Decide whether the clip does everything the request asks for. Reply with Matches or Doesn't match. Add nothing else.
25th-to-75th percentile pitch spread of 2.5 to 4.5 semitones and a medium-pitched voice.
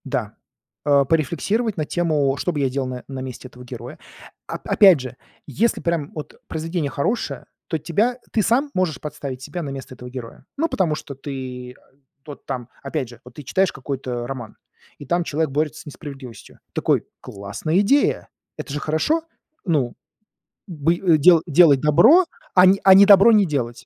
Doesn't match